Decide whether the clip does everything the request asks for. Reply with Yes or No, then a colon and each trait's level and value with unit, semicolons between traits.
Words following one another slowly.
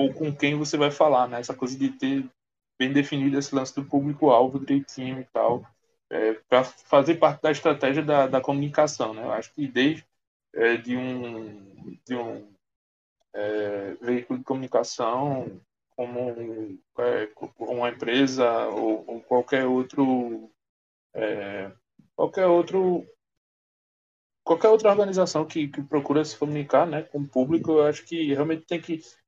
No: average, 150 wpm